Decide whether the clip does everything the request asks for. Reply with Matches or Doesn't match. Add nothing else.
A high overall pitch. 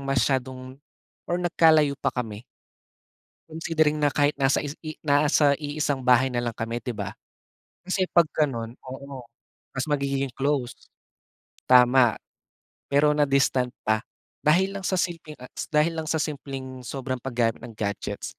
Doesn't match